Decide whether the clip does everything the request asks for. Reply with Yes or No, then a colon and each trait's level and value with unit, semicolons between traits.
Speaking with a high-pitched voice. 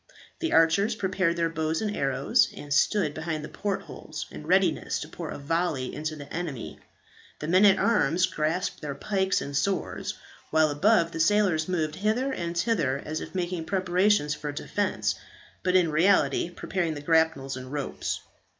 No: medium, 165 Hz